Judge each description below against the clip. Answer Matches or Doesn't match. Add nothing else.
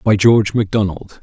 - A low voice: Matches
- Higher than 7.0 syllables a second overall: Doesn't match